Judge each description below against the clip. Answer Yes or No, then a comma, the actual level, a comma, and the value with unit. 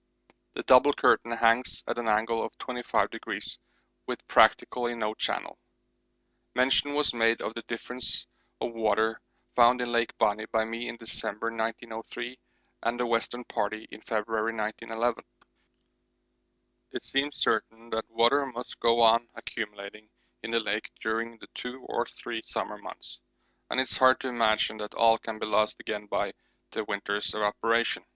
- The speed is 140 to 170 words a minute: Yes, average, 155 wpm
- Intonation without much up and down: Yes, narrow, 1.5 semitones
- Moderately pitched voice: No, low, 115 Hz